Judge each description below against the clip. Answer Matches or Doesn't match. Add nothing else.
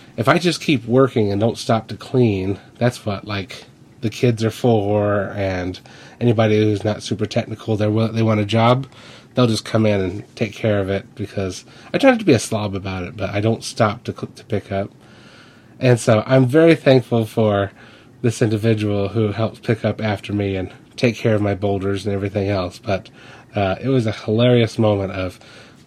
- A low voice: Matches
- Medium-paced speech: Matches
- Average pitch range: Matches